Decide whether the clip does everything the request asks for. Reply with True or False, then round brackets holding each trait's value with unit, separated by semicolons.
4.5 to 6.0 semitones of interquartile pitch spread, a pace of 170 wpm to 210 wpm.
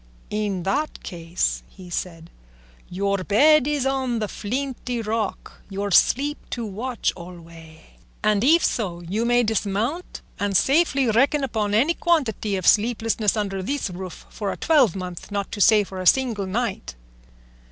False (5.0 semitones; 150 wpm)